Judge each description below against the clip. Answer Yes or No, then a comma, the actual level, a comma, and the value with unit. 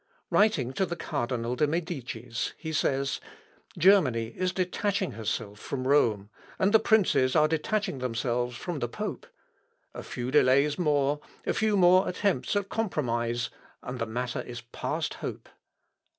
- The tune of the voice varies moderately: No, wide, 7.0 semitones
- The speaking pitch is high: No, medium, 140 Hz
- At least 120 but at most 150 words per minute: Yes, average, 145 wpm